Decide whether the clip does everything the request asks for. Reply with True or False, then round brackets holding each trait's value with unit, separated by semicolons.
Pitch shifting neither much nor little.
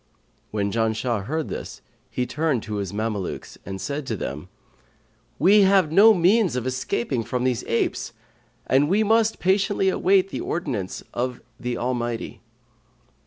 False (8.7 semitones)